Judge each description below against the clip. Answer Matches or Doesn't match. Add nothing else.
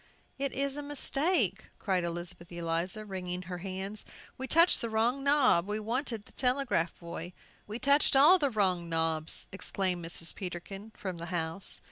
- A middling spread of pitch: Doesn't match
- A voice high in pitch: Matches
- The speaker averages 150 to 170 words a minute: Matches